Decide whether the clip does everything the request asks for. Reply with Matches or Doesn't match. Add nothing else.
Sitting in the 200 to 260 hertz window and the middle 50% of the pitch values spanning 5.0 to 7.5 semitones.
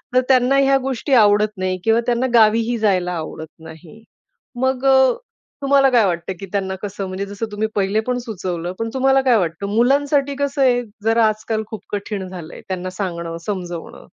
Matches